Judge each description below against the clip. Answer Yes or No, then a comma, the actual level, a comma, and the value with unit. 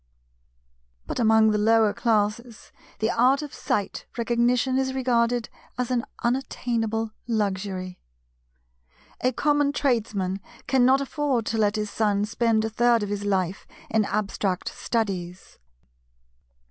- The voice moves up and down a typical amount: Yes, average, 3.0 semitones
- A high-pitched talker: Yes, high, 225 Hz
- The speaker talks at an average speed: No, slow, 120 wpm